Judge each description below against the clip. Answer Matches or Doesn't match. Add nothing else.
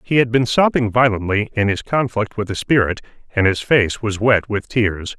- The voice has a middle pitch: Doesn't match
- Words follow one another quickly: Matches